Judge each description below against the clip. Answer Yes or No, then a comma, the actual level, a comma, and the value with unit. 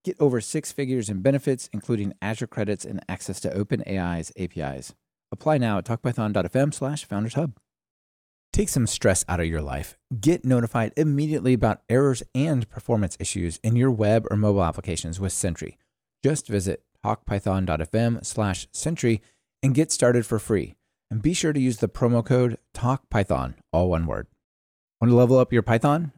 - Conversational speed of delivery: Yes, average, 165 wpm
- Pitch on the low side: Yes, low, 115 Hz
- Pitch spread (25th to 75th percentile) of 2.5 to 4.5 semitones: No, average, 5.3 semitones